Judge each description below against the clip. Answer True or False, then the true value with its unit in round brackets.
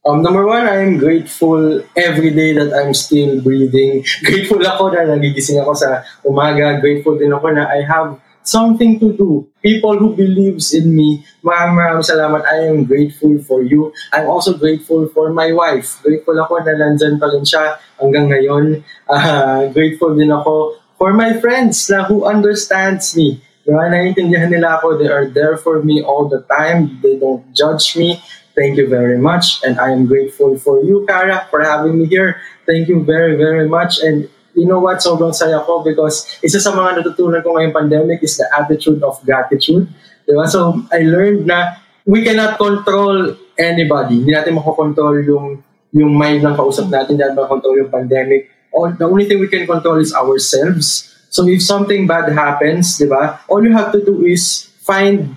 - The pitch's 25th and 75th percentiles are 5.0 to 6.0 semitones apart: False (3.7 semitones)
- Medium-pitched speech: True (160 Hz)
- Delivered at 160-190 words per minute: True (170 wpm)